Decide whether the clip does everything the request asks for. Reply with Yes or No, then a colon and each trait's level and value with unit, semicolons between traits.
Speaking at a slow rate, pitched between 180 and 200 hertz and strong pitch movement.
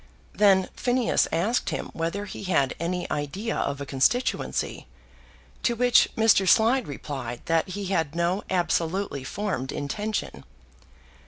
Yes: slow, 130 wpm; medium, 185 Hz; wide, 6.2 semitones